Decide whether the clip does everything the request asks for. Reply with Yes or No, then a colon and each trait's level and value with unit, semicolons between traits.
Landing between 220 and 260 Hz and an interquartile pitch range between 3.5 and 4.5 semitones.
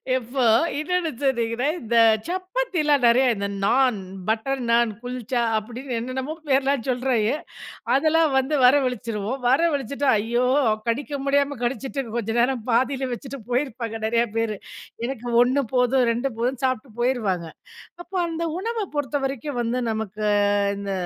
No: very high, 255 Hz; average, 3.1 semitones